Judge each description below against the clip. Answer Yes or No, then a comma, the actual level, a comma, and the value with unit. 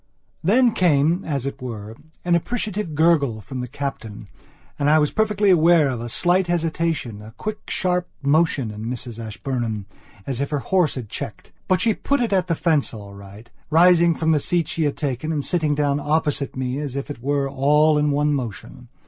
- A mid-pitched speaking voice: Yes, medium, 150 Hz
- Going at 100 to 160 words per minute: No, average, 190 wpm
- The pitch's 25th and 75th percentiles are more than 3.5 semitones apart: Yes, average, 5.1 semitones